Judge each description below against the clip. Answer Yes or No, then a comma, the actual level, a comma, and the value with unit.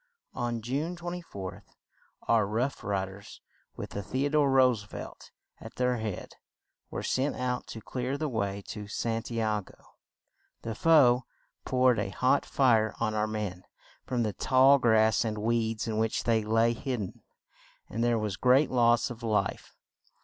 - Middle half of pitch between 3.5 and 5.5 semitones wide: No, average, 3.0 semitones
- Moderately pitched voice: No, low, 115 Hz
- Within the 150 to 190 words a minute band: Yes, average, 165 wpm